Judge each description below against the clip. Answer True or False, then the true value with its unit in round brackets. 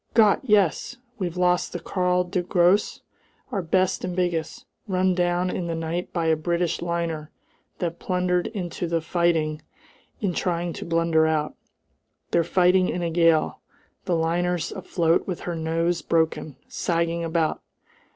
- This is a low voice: False (175 Hz)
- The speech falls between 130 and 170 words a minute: True (150 wpm)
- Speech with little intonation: True (1.5 semitones)